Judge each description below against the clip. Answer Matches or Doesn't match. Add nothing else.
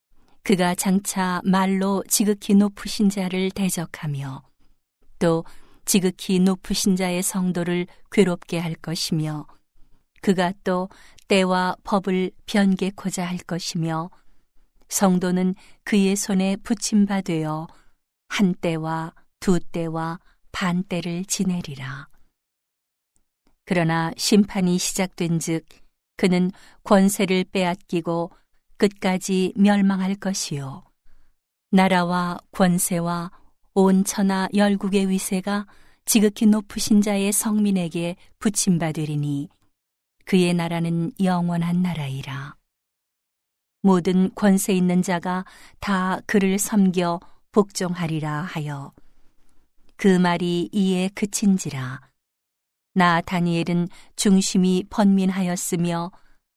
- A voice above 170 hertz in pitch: Matches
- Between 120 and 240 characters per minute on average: Matches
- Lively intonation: Doesn't match